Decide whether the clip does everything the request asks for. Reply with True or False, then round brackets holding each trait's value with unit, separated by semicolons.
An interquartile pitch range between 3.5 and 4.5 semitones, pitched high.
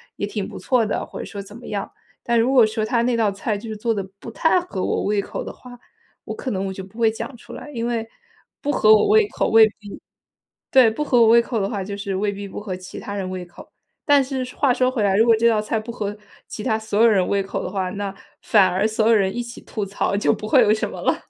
False (2.8 semitones; 220 Hz)